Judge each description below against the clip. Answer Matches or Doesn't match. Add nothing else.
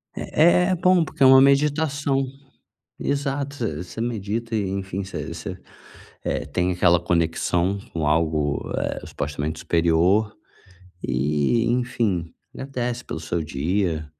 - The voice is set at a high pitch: Doesn't match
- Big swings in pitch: Matches